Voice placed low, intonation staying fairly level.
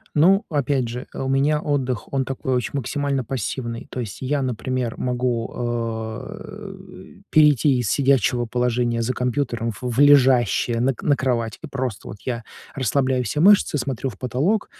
No: low, 130 Hz; average, 3.0 semitones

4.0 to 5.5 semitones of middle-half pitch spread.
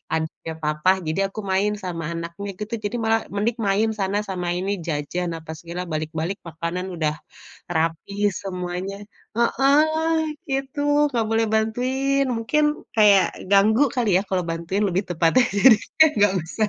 Yes: average, 5.0 semitones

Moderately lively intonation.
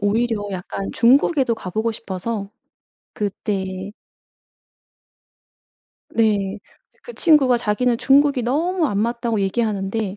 Yes: average, 3.6 semitones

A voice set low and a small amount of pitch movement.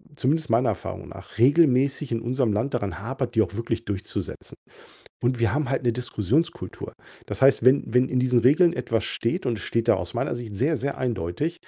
No: low, 125 Hz; average, 3.2 semitones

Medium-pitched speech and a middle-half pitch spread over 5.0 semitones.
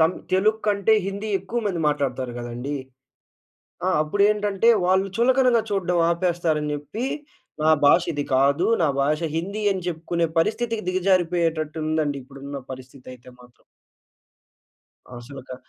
Yes: medium, 170 Hz; wide, 5.6 semitones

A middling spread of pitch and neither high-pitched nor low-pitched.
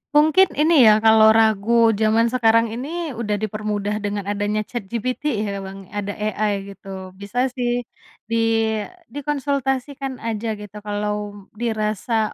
No: average, 3.1 semitones; high, 220 Hz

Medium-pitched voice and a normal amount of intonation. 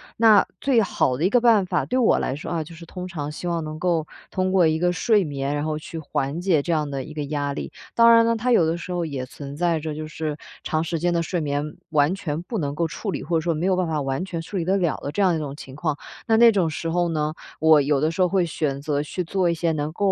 Yes: medium, 165 Hz; average, 3.3 semitones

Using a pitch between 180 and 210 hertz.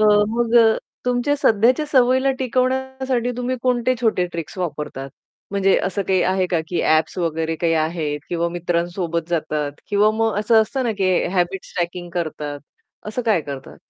Yes: high, 190 Hz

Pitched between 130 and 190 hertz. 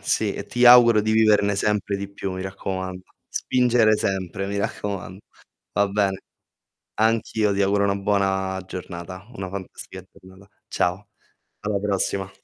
No: low, 100 Hz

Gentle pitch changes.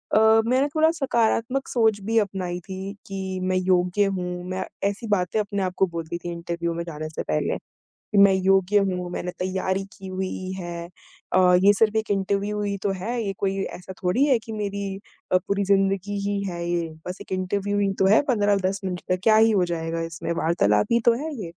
Yes: narrow, 2.3 semitones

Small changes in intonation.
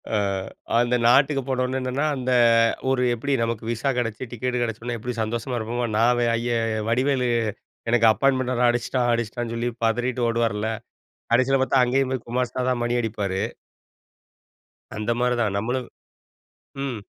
Yes: narrow, 1.8 semitones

